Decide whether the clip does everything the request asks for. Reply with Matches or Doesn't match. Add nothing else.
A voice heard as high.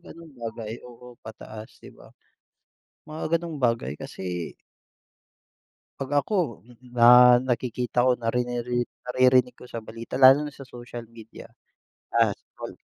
Doesn't match